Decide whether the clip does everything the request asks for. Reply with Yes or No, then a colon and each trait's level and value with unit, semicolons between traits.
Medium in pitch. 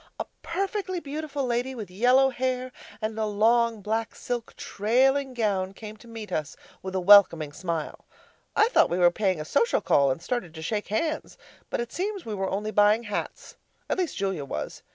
No: high, 220 Hz